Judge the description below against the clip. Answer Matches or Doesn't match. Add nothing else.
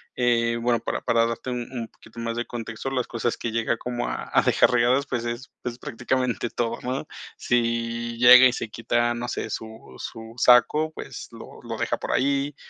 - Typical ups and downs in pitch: Doesn't match